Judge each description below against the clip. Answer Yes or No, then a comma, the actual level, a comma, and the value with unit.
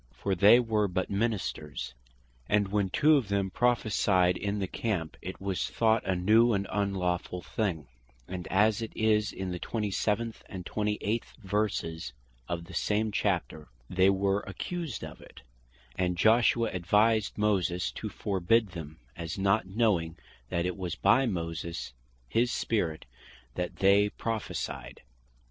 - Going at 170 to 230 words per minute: No, average, 145 wpm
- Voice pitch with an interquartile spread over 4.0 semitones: No, average, 3.3 semitones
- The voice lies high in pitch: No, low, 100 Hz